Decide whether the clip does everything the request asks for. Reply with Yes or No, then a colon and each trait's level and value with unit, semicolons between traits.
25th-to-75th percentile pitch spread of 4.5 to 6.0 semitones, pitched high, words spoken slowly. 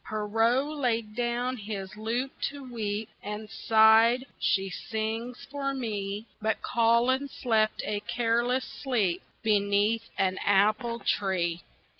No: average, 2.8 semitones; high, 225 Hz; slow, 115 wpm